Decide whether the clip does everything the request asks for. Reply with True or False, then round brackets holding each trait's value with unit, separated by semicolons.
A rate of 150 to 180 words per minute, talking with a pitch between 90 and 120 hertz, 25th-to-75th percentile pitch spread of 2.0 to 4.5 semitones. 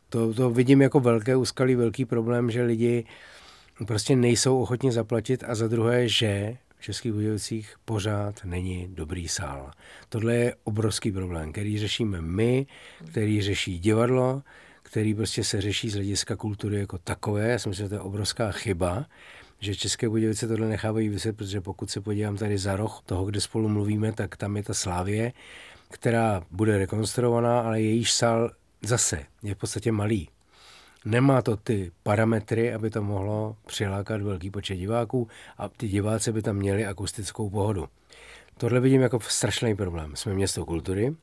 True (165 wpm; 110 Hz; 2.5 semitones)